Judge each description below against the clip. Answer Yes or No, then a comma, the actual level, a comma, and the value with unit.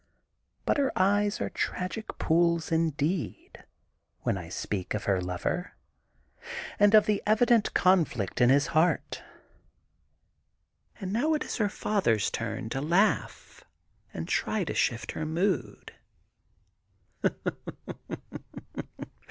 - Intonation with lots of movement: Yes, wide, 8.6 semitones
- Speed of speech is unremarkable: No, slow, 110 wpm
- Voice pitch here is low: No, medium, 170 Hz